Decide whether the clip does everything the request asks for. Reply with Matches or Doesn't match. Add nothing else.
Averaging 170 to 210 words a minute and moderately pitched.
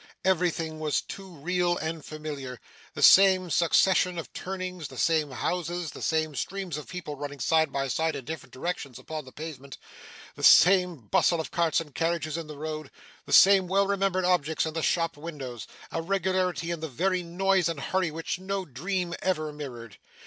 Matches